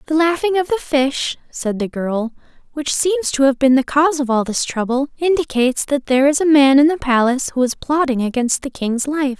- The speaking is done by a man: No, female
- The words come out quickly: Yes, fast, 225 wpm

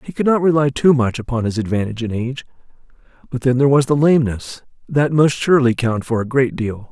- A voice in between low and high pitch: No, low, 130 Hz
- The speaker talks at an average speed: No, fast, 215 wpm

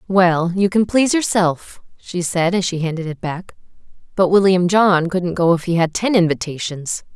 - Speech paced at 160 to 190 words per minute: Yes, average, 185 wpm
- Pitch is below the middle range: No, medium, 180 Hz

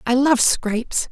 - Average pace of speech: Yes, average, 160 wpm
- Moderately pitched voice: No, very high, 250 Hz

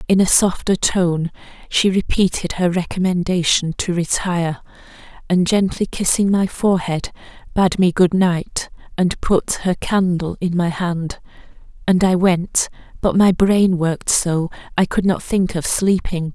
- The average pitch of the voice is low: No, medium, 180 Hz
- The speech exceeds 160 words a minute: No, average, 145 wpm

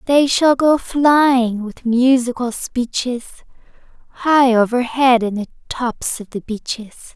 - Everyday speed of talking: No, slow, 125 wpm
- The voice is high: Yes, very high, 250 Hz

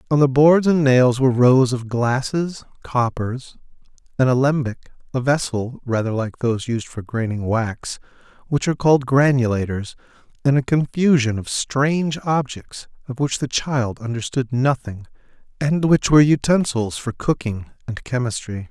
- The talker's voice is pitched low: Yes, low, 130 Hz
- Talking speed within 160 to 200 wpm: No, average, 145 wpm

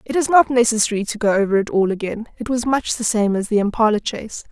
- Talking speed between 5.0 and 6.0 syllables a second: No, 6.4 syllables/s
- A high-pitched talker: Yes, high, 220 Hz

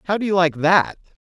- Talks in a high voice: No, medium, 175 Hz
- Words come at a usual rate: No, fast, 235 wpm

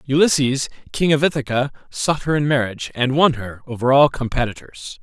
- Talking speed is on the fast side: No, average, 165 wpm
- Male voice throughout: Yes, male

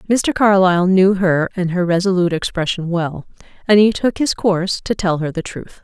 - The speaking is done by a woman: Yes, female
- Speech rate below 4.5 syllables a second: No, 5.3 syllables/s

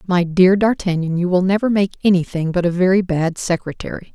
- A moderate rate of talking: Yes, average, 190 wpm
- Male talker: No, female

